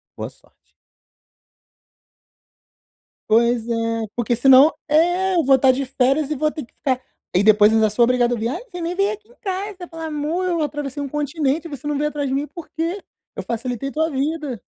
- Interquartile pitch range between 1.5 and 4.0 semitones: No, average, 4.6 semitones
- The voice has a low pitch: No, very high, 290 Hz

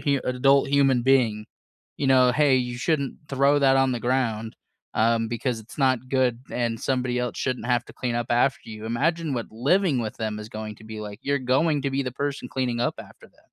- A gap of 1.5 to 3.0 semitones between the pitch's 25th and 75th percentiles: Yes, average, 2.7 semitones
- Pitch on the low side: Yes, low, 125 Hz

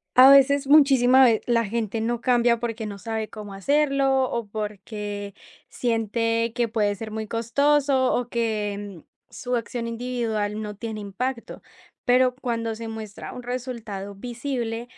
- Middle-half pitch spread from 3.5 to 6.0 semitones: No, average, 2.7 semitones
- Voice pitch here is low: No, high, 230 Hz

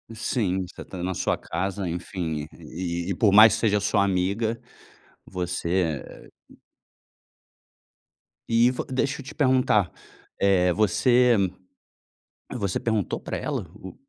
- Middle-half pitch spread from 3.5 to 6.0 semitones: Yes, average, 3.9 semitones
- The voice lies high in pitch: No, low, 100 Hz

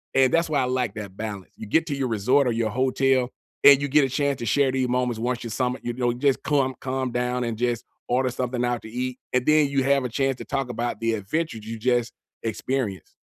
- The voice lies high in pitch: No, low, 125 Hz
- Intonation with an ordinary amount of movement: No, narrow, 2.3 semitones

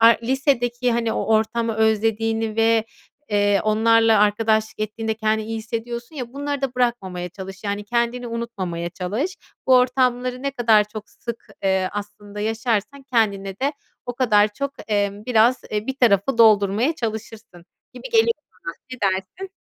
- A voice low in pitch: No, high, 225 Hz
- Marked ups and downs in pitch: No, average, 2.8 semitones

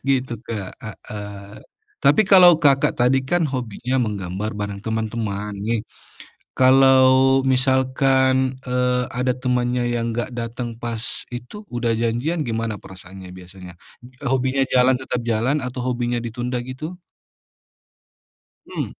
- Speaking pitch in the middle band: No, low, 125 Hz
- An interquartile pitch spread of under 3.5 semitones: Yes, average, 2.9 semitones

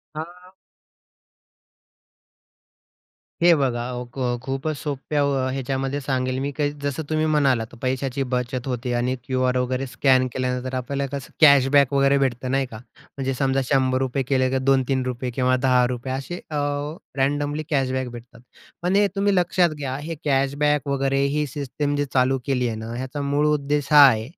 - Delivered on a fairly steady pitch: Yes, narrow, 2.1 semitones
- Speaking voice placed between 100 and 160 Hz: Yes, low, 135 Hz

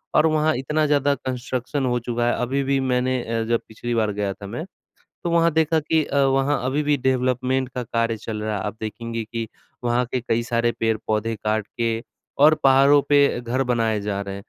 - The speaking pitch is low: Yes, low, 125 Hz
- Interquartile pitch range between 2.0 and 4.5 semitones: Yes, average, 3.4 semitones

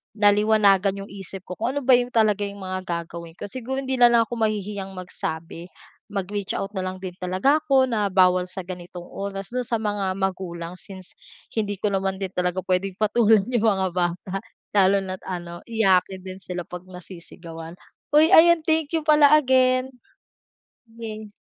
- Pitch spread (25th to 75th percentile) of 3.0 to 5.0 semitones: Yes, average, 3.6 semitones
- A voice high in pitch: Yes, high, 195 Hz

